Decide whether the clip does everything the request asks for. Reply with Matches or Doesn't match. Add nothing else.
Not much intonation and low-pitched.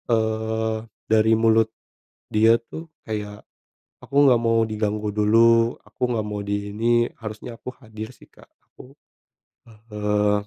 Matches